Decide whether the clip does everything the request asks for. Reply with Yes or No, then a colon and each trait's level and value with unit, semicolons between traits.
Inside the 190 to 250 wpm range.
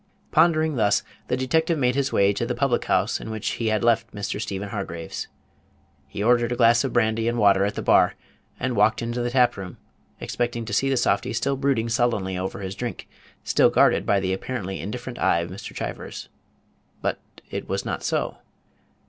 Yes: average, 195 wpm